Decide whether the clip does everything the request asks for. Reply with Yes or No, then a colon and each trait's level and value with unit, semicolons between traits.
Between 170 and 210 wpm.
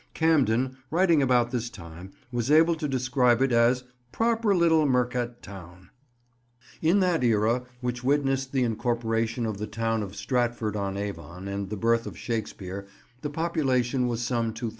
No: average, 160 wpm